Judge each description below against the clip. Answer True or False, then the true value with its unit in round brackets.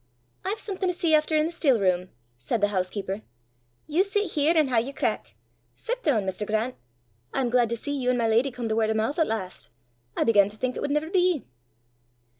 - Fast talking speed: True (225 wpm)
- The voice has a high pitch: True (250 Hz)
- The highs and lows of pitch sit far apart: True (6.4 semitones)